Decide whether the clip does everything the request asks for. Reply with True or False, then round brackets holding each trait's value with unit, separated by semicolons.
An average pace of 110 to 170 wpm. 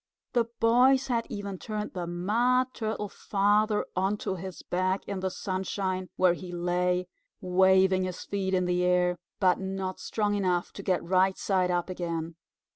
True (160 wpm)